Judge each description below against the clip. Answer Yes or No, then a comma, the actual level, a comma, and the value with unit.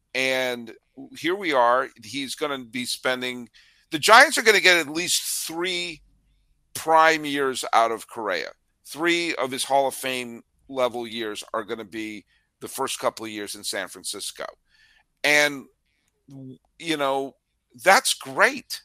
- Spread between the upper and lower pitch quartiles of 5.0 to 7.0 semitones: Yes, wide, 5.5 semitones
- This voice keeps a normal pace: Yes, average, 155 wpm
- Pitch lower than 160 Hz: Yes, low, 135 Hz